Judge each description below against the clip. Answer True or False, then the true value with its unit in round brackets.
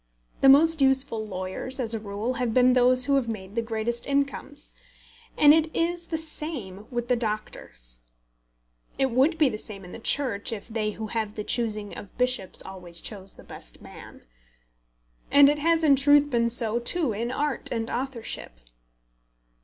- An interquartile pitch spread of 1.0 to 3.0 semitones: False (4.6 semitones)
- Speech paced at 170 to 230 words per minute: True (175 wpm)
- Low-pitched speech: False (240 Hz)